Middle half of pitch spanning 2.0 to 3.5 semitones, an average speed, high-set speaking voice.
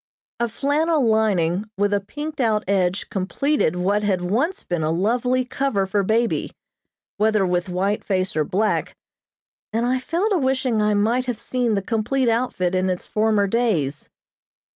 No: average, 4.7 semitones; average, 165 wpm; high, 215 Hz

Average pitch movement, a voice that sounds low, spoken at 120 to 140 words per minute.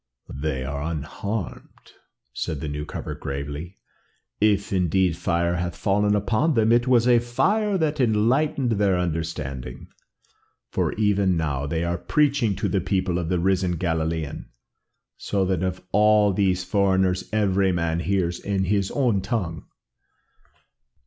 Yes: average, 4.1 semitones; very low, 95 Hz; slow, 135 wpm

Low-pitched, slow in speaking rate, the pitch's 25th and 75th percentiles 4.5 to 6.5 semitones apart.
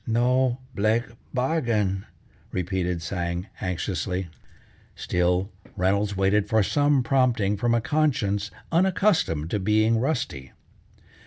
Yes: low, 105 Hz; slow, 100 wpm; average, 5.1 semitones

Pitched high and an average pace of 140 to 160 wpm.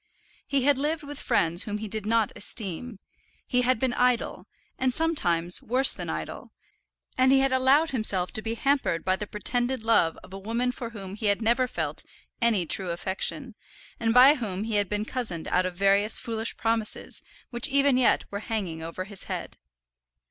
No: high, 225 Hz; average, 185 wpm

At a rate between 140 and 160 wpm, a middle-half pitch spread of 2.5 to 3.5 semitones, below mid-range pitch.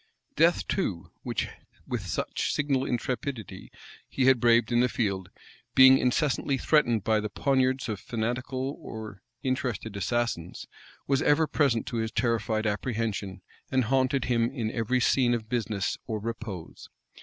Yes: average, 145 wpm; average, 3.2 semitones; low, 120 Hz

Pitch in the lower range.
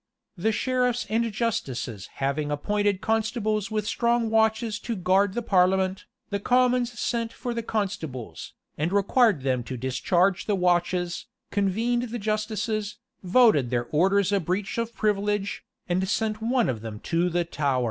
No: high, 205 Hz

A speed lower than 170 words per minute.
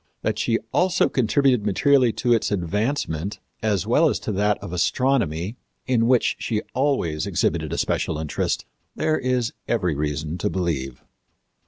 Yes: average, 150 wpm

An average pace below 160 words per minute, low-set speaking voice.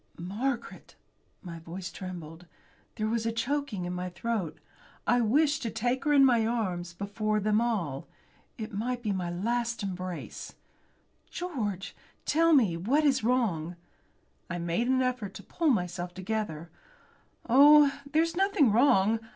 No: average, 145 wpm; high, 220 Hz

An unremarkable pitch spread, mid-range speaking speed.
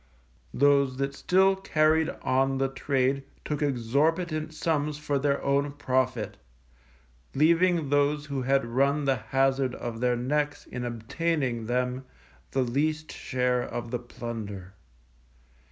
No: average, 3.2 semitones; slow, 125 wpm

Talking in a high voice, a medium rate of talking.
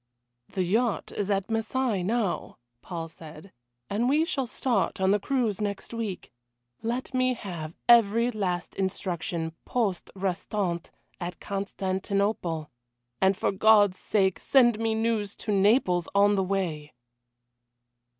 No: high, 200 Hz; slow, 130 wpm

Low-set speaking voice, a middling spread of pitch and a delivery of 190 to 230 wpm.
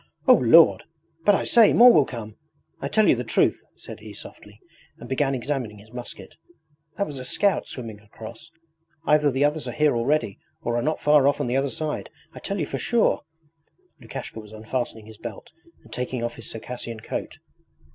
Yes: low, 130 Hz; average, 4.7 semitones; average, 195 wpm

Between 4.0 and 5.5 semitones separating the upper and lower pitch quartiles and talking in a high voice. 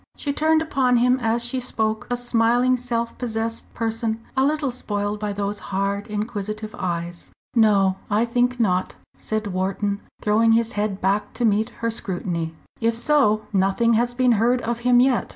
No: average, 2.9 semitones; high, 225 Hz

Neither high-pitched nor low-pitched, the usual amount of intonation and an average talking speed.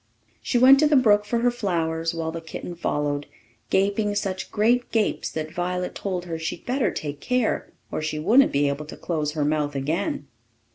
No: medium, 175 Hz; wide, 5.8 semitones; average, 190 wpm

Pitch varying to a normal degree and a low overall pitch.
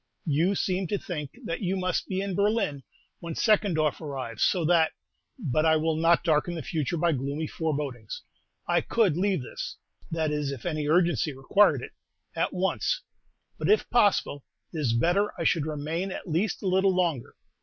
No: average, 3.9 semitones; medium, 165 Hz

